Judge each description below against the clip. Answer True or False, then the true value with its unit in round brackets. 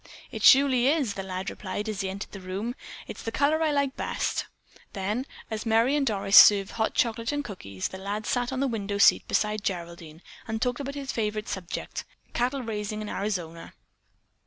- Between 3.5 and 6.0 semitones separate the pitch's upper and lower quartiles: True (4.3 semitones)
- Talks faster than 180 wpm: True (190 wpm)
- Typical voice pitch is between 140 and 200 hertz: False (215 Hz)